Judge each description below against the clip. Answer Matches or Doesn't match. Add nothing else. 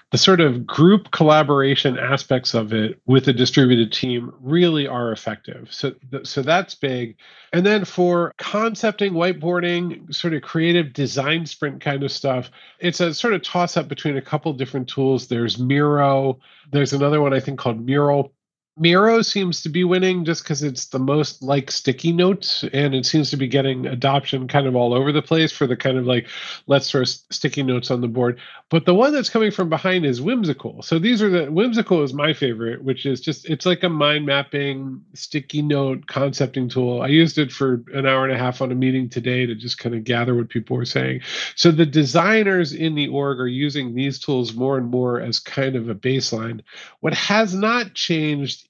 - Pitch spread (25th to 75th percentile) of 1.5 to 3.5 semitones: Doesn't match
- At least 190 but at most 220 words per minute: Matches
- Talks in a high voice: Doesn't match